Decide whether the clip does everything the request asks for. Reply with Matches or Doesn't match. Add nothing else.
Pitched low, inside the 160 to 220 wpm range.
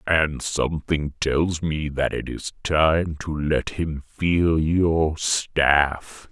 Doesn't match